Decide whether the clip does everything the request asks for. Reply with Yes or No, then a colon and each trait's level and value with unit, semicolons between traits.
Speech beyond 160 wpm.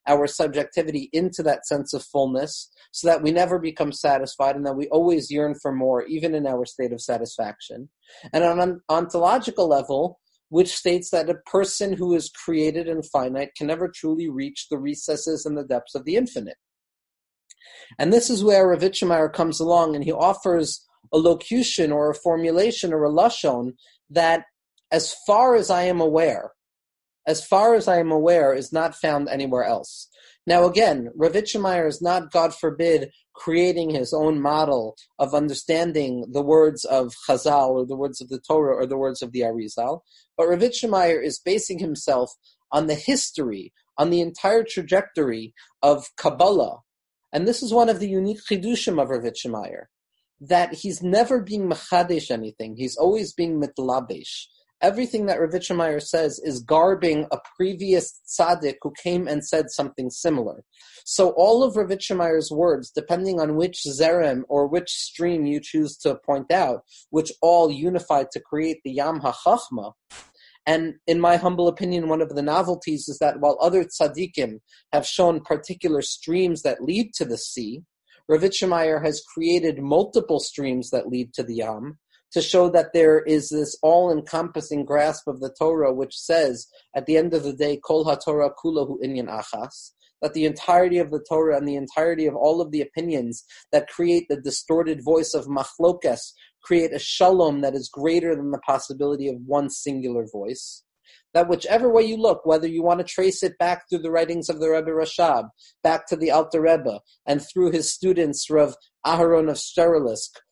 Yes: average, 170 wpm